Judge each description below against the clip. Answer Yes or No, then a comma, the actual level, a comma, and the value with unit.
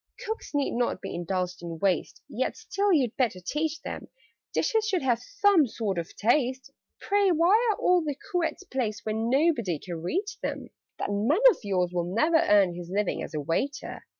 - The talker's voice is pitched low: No, very high, 250 Hz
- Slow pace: No, average, 185 wpm